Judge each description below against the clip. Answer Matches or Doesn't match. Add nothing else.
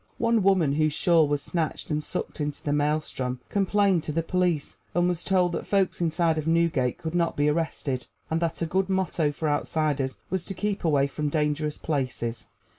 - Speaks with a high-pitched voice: Doesn't match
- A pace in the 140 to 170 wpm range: Doesn't match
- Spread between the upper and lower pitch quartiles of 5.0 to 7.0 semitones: Doesn't match